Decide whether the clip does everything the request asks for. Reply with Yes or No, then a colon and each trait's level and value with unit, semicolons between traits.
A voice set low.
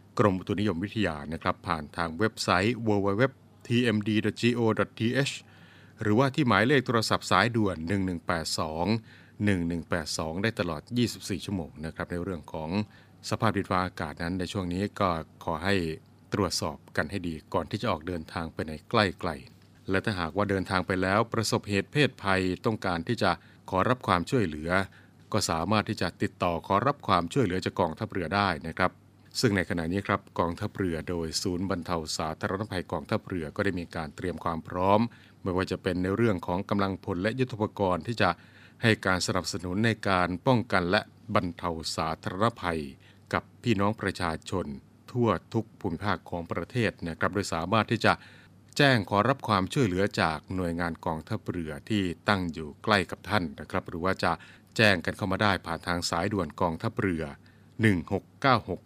Yes: very low, 95 Hz